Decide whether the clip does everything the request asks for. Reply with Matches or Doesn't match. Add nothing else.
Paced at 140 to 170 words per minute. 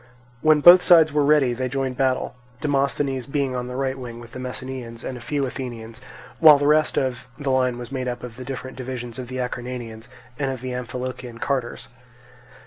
Doesn't match